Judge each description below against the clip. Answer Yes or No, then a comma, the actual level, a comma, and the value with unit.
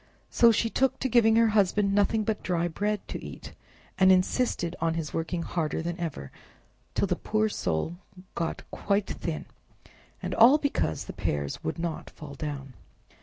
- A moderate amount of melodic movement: Yes, average, 5.0 semitones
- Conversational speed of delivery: Yes, average, 170 wpm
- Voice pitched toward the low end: No, medium, 185 Hz